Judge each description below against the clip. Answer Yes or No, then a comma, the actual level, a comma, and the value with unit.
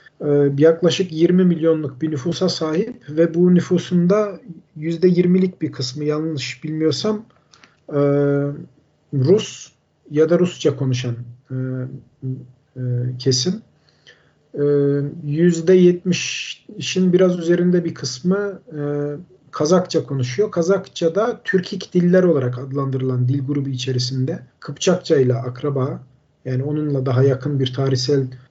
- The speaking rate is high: No, slow, 95 wpm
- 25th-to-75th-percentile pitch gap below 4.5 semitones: No, average, 4.8 semitones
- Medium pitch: Yes, medium, 150 Hz